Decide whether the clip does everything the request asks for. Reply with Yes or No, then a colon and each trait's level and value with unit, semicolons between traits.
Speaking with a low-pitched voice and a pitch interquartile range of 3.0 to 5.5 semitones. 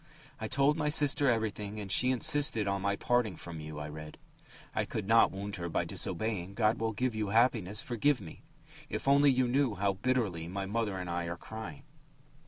Yes: low, 105 Hz; average, 4.7 semitones